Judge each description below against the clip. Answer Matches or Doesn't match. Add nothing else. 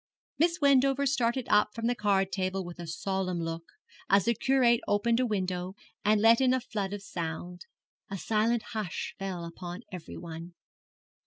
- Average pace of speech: Matches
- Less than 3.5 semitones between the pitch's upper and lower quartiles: Doesn't match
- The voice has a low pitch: Doesn't match